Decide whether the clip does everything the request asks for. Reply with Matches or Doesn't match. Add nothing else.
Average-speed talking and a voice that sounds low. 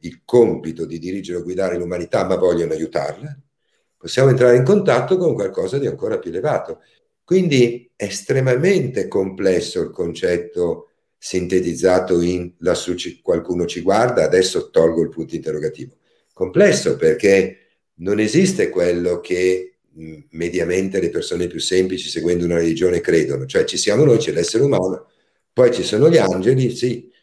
Matches